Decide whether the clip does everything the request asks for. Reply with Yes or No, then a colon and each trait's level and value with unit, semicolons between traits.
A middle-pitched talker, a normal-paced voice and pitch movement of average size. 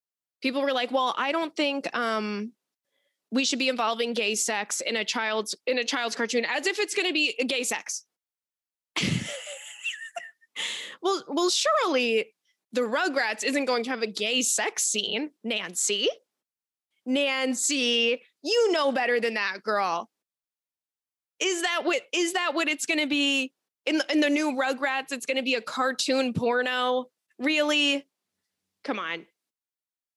No: very high, 265 Hz; average, 145 wpm; average, 4.3 semitones